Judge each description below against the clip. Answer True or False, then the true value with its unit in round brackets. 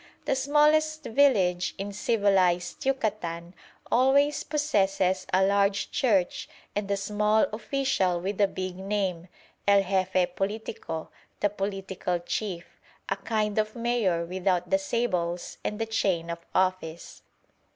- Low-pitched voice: False (195 Hz)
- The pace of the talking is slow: True (125 wpm)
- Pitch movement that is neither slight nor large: True (3.2 semitones)